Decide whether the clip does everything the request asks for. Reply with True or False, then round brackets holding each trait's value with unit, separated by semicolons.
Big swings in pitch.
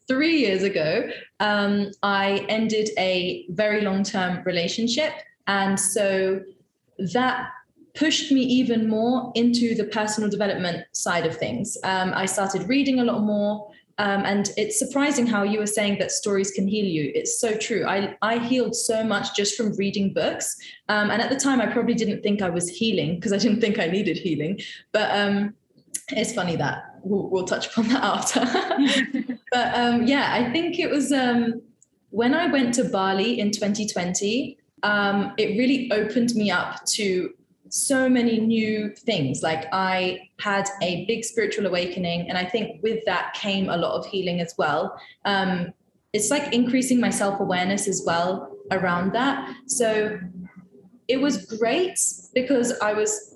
False (3.8 semitones)